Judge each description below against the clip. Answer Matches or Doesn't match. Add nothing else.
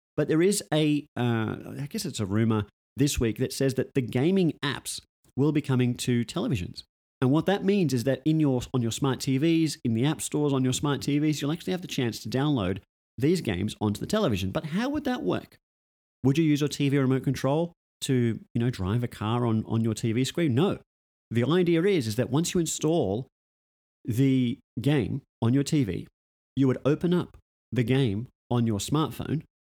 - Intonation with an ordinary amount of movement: Matches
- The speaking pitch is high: Doesn't match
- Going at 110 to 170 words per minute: Doesn't match